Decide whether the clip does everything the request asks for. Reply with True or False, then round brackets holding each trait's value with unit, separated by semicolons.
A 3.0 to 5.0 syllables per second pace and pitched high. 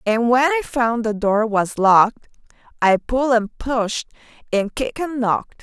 True (4.5 syllables/s; 235 Hz)